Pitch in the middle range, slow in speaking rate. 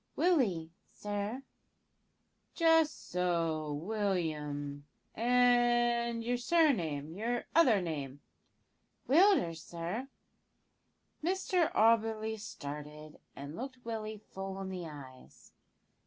No: high, 210 Hz; slow, 85 wpm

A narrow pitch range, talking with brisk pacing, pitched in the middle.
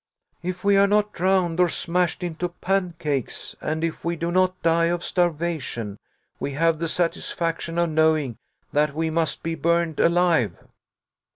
No: narrow, 2.0 semitones; average, 155 wpm; medium, 170 Hz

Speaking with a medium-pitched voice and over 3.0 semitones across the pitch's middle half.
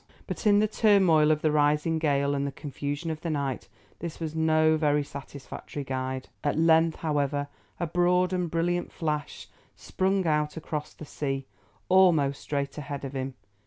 No: medium, 150 Hz; average, 2.7 semitones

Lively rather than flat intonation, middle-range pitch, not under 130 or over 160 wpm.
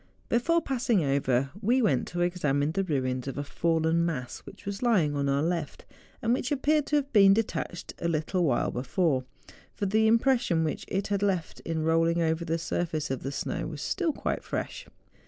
No: wide, 6.7 semitones; medium, 170 Hz; average, 195 wpm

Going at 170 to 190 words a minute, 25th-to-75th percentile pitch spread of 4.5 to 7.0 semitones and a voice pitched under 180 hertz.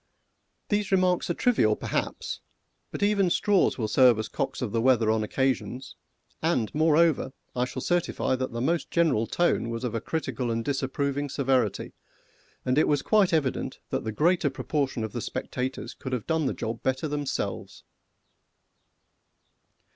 No: average, 160 wpm; average, 5.3 semitones; low, 135 Hz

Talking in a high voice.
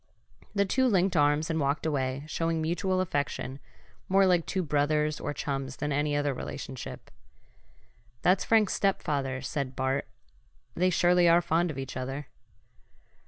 No: medium, 150 Hz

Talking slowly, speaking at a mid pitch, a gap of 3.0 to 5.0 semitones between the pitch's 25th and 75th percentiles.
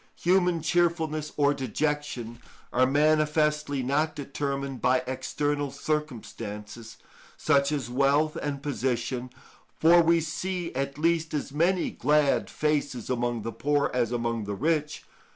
Yes: slow, 125 wpm; medium, 145 Hz; average, 3.3 semitones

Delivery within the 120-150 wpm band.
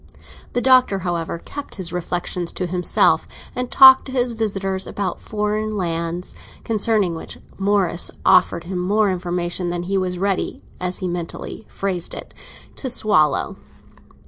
Yes: average, 145 wpm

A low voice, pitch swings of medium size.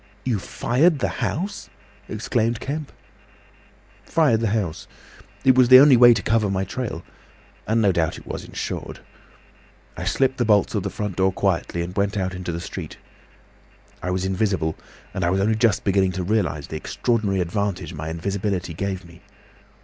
Yes: low, 100 Hz; average, 4.1 semitones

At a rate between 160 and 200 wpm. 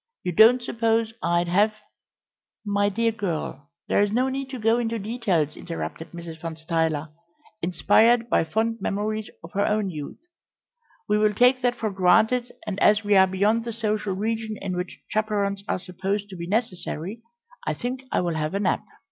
Yes: average, 180 wpm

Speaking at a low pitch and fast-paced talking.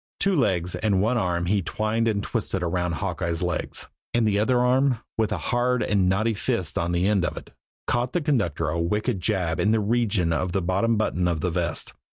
Yes: low, 100 Hz; fast, 210 wpm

